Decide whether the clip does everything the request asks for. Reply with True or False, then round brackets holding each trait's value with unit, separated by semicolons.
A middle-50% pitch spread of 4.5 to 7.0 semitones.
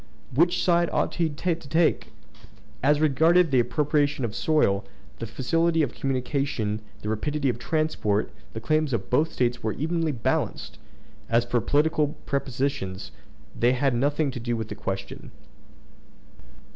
True (4.8 semitones)